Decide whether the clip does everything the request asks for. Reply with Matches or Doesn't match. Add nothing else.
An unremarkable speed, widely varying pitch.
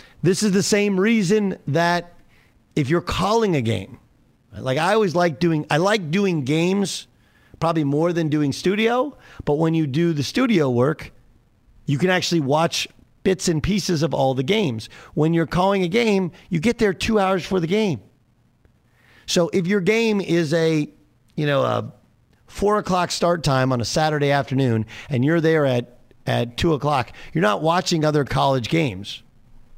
Matches